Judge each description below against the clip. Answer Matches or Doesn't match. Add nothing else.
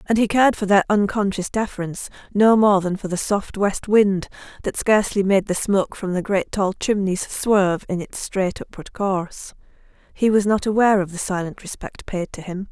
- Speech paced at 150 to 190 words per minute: Doesn't match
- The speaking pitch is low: Doesn't match